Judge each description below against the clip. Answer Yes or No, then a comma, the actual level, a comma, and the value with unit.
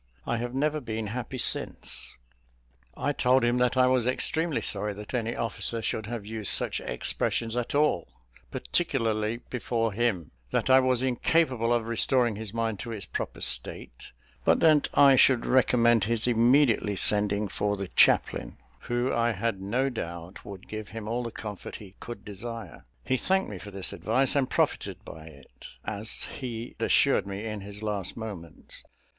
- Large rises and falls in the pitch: No, average, 3.3 semitones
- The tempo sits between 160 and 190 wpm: Yes, average, 170 wpm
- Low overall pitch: Yes, low, 115 Hz